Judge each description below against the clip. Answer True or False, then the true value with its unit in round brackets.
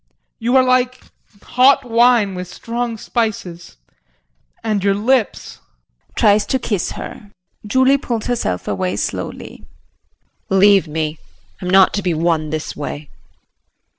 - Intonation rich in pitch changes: True (6.0 semitones)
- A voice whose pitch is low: False (205 Hz)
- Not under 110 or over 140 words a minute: True (135 wpm)